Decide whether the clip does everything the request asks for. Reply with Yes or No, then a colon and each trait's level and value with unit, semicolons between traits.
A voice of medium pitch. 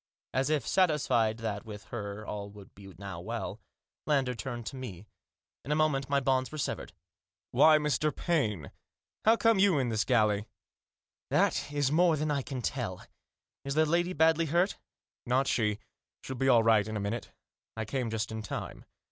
No: low, 130 Hz